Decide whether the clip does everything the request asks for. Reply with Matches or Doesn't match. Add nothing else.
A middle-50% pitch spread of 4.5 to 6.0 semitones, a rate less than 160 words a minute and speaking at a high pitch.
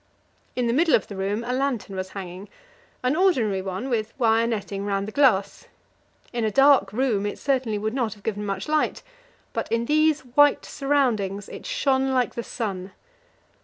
Doesn't match